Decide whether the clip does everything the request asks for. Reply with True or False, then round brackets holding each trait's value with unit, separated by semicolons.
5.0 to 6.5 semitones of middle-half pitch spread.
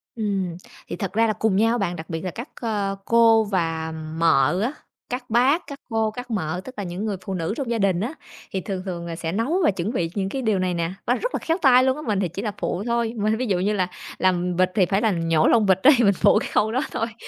False (4.3 semitones)